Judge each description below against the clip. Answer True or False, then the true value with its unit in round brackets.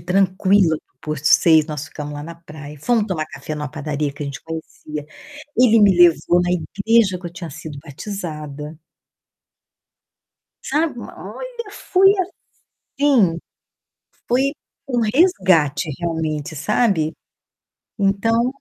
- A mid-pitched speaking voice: True (170 Hz)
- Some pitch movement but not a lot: False (6.1 semitones)